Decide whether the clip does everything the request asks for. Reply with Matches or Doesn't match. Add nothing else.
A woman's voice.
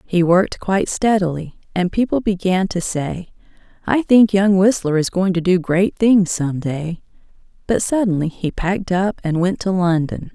Matches